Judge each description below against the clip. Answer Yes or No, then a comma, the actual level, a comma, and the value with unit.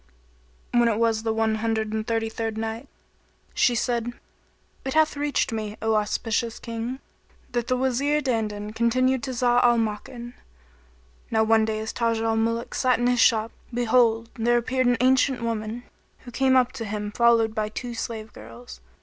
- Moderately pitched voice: No, high, 230 Hz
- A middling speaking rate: Yes, average, 175 wpm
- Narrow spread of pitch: Yes, narrow, 1.9 semitones